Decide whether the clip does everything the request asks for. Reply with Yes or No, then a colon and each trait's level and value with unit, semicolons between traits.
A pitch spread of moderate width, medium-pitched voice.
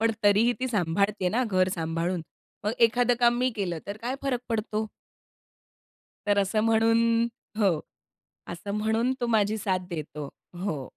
No: average, 3.8 semitones; high, 210 Hz